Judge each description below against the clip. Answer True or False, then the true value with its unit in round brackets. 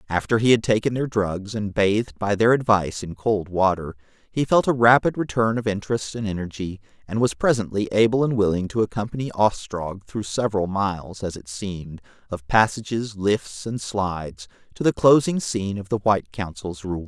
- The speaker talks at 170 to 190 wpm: True (185 wpm)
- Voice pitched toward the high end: False (105 Hz)